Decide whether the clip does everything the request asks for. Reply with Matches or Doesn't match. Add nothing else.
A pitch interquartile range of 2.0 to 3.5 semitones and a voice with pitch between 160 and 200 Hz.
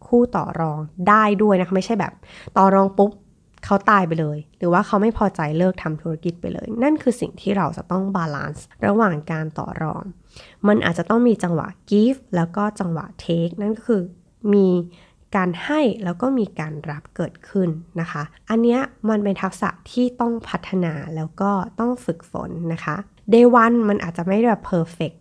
Doesn't match